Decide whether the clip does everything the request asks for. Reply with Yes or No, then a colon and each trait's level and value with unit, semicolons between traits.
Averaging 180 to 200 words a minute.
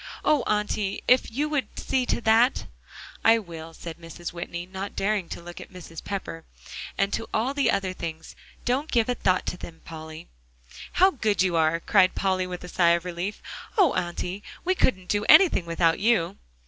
Yes: average, 185 wpm